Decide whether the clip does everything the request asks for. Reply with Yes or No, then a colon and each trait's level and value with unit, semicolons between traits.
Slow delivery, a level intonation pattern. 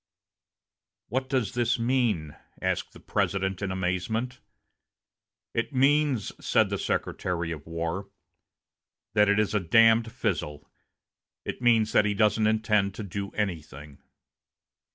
No: slow, 125 wpm; average, 3.9 semitones